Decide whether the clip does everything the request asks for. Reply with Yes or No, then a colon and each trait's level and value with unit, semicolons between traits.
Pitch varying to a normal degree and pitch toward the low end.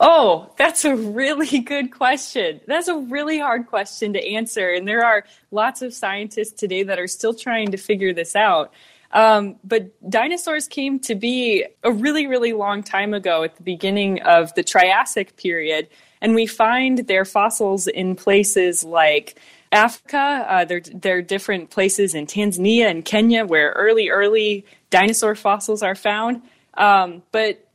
No: average, 3.7 semitones; high, 215 Hz